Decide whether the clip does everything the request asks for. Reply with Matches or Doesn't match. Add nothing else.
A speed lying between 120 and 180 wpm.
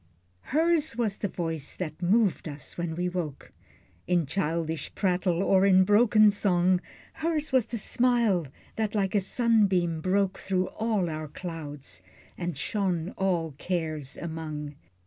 Matches